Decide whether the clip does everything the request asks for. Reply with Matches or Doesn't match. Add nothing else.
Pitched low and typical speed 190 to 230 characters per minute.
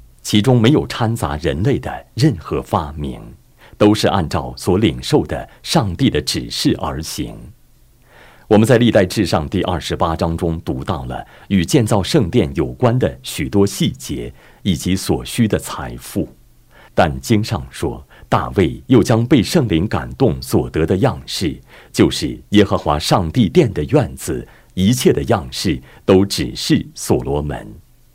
Matches